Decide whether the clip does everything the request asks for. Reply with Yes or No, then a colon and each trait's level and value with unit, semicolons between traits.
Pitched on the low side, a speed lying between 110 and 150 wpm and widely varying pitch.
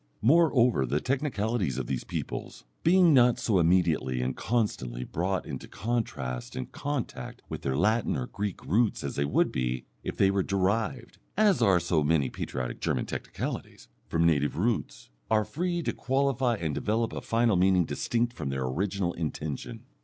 No: very low, 95 Hz; average, 165 wpm; wide, 8.5 semitones